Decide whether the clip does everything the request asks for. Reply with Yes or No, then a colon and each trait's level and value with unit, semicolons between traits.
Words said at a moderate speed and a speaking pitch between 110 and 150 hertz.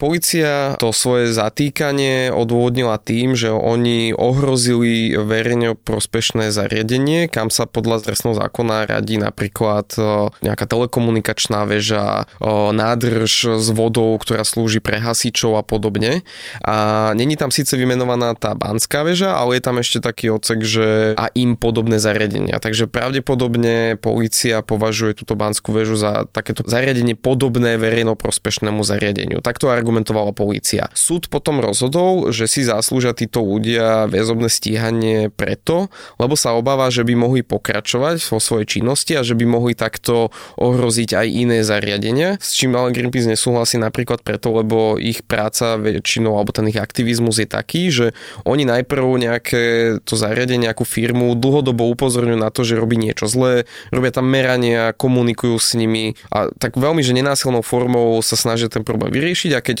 Yes: average, 150 wpm; low, 115 Hz